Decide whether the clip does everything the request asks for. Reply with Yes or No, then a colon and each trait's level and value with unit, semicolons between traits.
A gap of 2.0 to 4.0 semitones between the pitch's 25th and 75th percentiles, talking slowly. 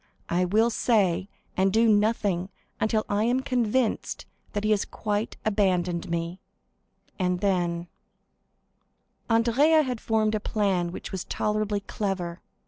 Yes: average, 3.5 semitones; slow, 130 wpm